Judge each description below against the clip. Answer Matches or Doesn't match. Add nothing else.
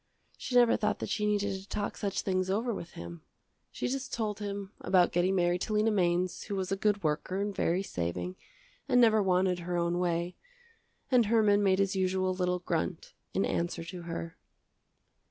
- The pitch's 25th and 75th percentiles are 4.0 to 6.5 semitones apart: Doesn't match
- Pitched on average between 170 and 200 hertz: Matches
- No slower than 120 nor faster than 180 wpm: Doesn't match